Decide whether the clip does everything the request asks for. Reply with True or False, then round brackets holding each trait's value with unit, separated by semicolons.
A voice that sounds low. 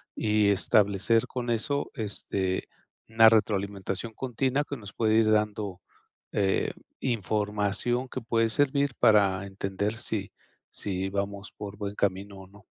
True (105 Hz)